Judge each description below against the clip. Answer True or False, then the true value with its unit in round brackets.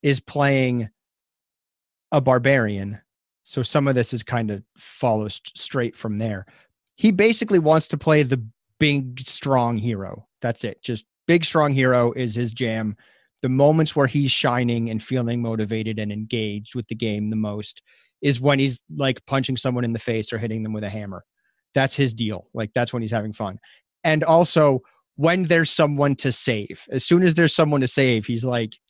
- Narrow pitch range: False (4.1 semitones)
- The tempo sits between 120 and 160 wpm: False (185 wpm)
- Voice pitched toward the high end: False (125 Hz)